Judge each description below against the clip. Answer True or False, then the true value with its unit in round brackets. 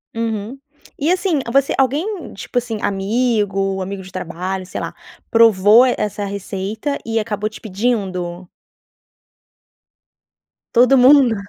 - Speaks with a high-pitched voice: True (215 Hz)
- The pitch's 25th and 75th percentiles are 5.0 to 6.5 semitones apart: False (4.4 semitones)